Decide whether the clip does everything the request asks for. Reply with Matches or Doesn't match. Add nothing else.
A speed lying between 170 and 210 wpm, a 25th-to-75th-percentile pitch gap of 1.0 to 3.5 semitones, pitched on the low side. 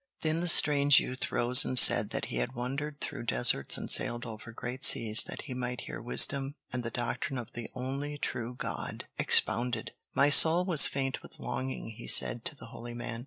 Matches